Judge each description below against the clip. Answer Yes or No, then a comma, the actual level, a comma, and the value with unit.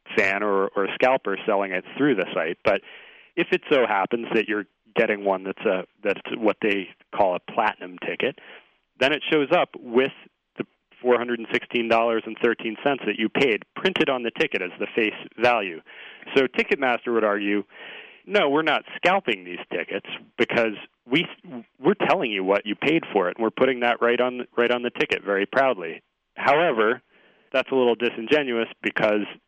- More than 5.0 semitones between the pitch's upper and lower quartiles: No, average, 2.9 semitones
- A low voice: Yes, low, 115 Hz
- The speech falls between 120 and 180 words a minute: No, average, 200 wpm